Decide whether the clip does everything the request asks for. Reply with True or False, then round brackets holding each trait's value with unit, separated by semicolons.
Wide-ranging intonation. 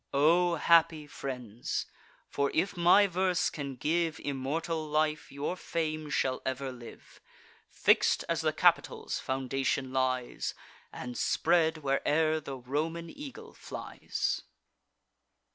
False (3.7 semitones)